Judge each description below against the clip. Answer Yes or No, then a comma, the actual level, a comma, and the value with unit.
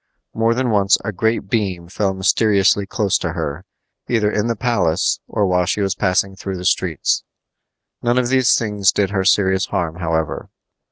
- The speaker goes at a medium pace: Yes, average, 175 wpm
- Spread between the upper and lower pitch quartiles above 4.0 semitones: No, average, 3.2 semitones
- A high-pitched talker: No, low, 100 Hz